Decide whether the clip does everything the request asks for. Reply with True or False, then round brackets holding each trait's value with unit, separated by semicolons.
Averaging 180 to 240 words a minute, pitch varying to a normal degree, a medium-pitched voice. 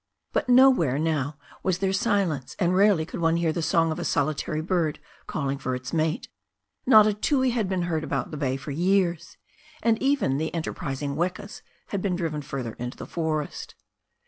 True (185 wpm; 4.4 semitones; 165 Hz)